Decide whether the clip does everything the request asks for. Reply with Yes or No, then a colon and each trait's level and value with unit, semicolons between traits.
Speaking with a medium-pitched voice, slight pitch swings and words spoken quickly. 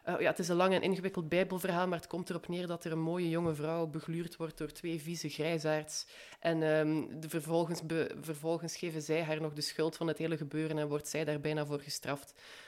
Yes: medium, 160 Hz; narrow, 1.7 semitones; fast, 230 wpm